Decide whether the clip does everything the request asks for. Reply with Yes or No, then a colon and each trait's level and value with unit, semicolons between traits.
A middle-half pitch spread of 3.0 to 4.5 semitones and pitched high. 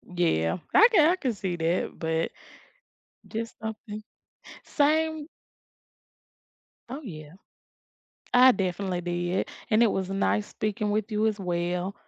No: average, 5.0 semitones; high, 205 Hz